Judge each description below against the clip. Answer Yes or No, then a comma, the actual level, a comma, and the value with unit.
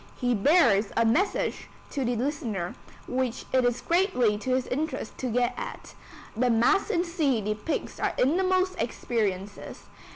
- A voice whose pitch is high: Yes, very high, 250 Hz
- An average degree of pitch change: No, wide, 5.9 semitones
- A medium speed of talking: Yes, average, 150 wpm